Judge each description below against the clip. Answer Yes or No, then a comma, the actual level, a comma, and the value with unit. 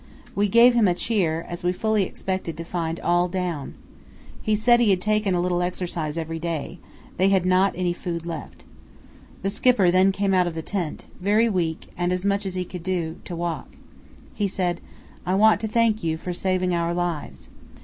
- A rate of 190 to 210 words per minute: Yes, average, 200 wpm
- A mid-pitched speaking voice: Yes, medium, 180 Hz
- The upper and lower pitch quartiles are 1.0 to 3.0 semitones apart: Yes, narrow, 2.5 semitones